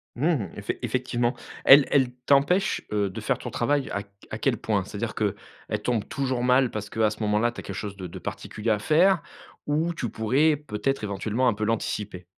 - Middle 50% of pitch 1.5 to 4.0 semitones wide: No, average, 4.7 semitones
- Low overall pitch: Yes, low, 120 Hz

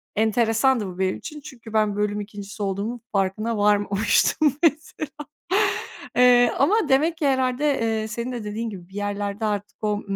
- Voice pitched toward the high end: Yes, high, 220 Hz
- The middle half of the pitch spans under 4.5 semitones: Yes, average, 3.7 semitones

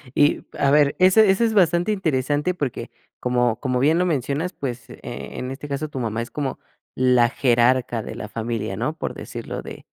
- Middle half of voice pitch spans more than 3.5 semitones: Yes, average, 4.6 semitones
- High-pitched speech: No, low, 135 Hz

